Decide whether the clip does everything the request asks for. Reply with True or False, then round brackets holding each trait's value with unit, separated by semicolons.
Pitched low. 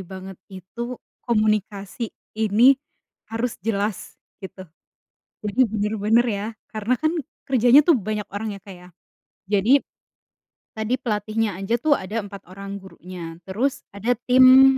False (215 Hz)